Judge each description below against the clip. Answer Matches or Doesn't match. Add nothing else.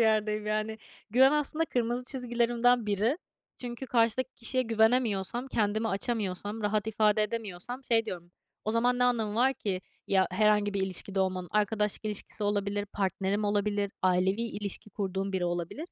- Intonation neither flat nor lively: Matches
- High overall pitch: Matches